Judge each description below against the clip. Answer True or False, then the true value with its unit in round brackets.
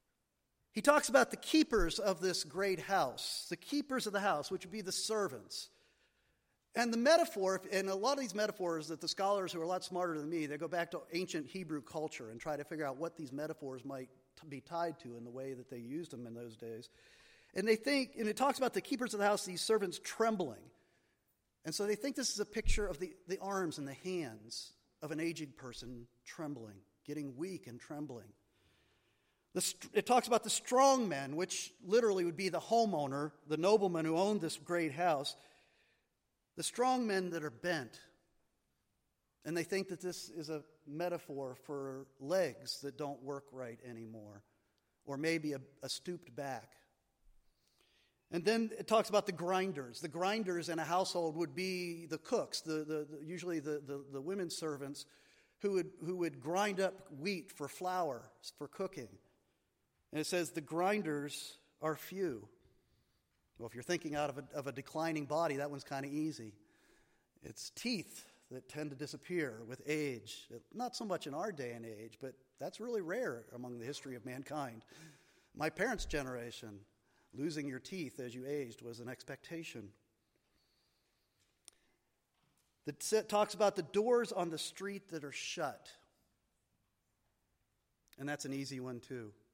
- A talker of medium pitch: True (160 Hz)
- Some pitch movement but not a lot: False (6.0 semitones)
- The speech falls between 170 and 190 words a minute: True (180 wpm)